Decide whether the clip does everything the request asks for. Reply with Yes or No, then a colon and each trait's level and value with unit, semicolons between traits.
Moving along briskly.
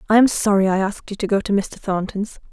Yes: fast, 260 wpm